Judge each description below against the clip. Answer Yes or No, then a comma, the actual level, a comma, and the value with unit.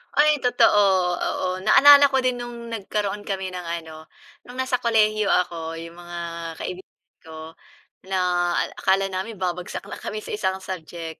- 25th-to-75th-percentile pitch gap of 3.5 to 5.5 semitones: Yes, average, 4.8 semitones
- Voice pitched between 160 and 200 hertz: Yes, high, 190 Hz